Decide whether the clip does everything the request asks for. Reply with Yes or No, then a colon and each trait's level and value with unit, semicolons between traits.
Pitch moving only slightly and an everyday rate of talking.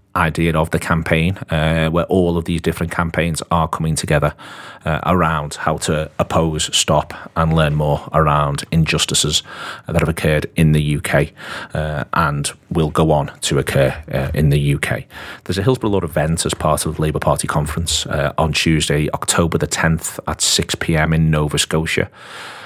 Yes: narrow, 1.6 semitones; average, 175 wpm